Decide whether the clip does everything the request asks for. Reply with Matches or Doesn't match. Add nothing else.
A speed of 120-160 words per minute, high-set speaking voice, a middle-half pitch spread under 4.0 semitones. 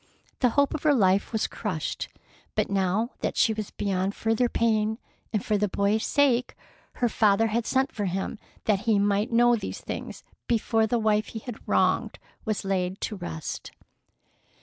Doesn't match